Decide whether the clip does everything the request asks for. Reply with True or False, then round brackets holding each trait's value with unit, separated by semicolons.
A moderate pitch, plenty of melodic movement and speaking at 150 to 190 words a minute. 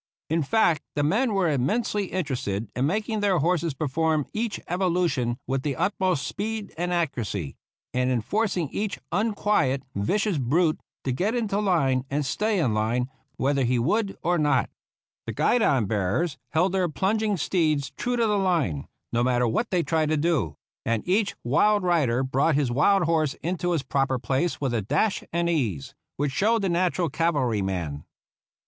True (160 Hz; 6.6 semitones; 170 wpm)